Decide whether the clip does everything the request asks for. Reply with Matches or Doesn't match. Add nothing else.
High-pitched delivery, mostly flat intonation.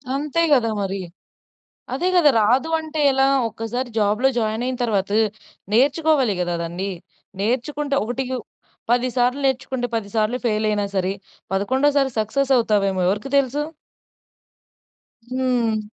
Doesn't match